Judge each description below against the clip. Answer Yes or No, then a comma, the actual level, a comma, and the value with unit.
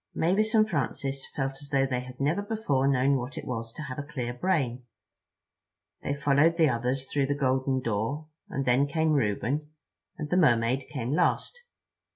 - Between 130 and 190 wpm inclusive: Yes, average, 180 wpm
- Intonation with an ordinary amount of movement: Yes, average, 3.0 semitones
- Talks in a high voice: No, low, 135 Hz